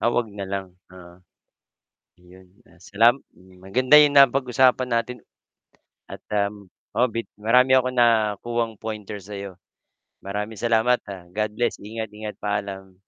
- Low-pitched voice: Yes, low, 110 Hz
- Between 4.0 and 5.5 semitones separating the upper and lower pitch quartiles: No, average, 3.5 semitones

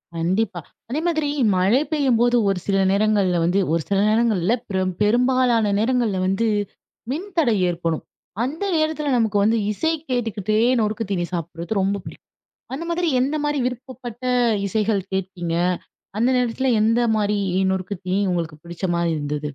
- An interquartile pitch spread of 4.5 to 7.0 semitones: Yes, average, 4.9 semitones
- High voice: Yes, high, 215 Hz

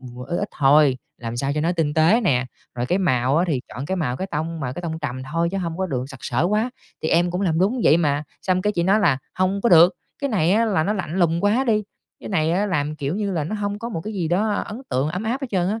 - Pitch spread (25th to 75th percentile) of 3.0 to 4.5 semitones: No, average, 5.3 semitones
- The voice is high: No, medium, 170 Hz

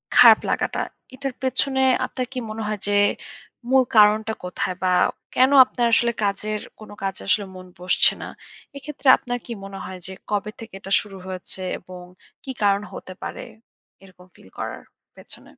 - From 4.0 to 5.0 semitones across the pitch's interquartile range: Yes, average, 4.4 semitones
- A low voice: No, high, 210 Hz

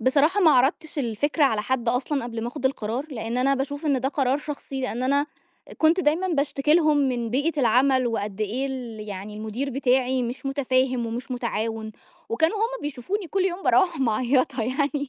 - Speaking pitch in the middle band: No, very high, 265 Hz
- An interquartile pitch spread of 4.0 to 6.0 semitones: No, average, 3.5 semitones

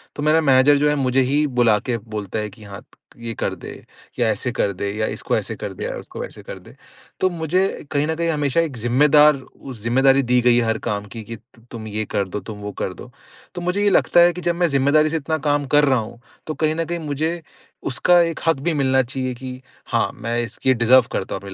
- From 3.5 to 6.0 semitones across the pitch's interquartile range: Yes, average, 5.1 semitones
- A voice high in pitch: No, low, 135 Hz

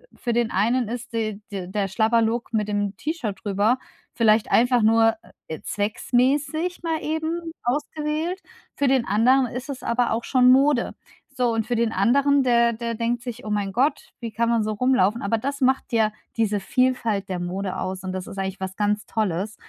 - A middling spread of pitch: Yes, average, 3.8 semitones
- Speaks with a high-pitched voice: Yes, high, 230 Hz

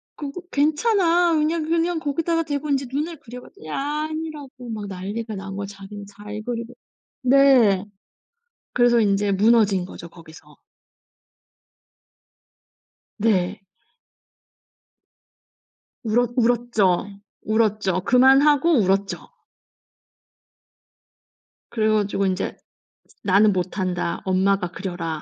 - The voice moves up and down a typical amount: No, wide, 6.4 semitones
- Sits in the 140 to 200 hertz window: No, high, 225 Hz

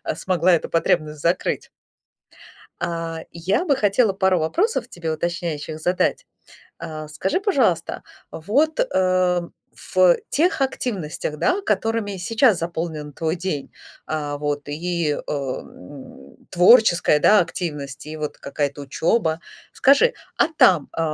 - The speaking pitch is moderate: Yes, medium, 175 Hz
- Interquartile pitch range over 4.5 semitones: Yes, average, 4.9 semitones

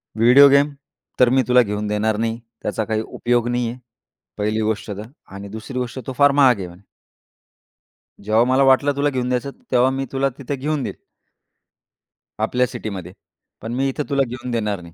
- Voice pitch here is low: Yes, low, 120 Hz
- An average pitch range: Yes, average, 3.6 semitones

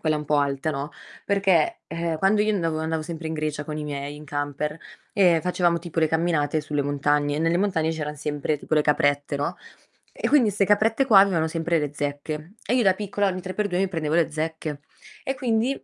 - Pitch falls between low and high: Yes, medium, 160 Hz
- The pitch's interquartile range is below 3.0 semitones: No, average, 3.9 semitones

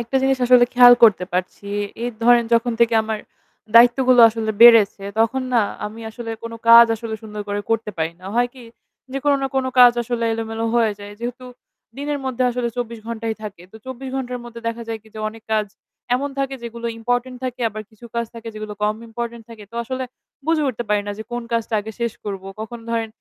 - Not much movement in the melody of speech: Yes, narrow, 1.8 semitones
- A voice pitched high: Yes, high, 235 Hz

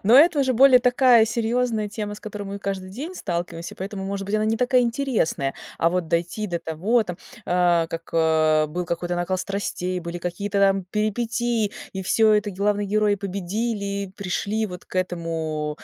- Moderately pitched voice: No, high, 200 Hz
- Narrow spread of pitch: No, average, 3.9 semitones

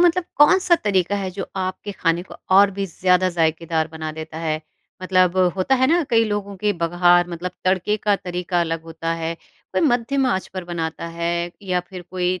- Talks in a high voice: No, medium, 180 Hz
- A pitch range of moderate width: Yes, average, 3.1 semitones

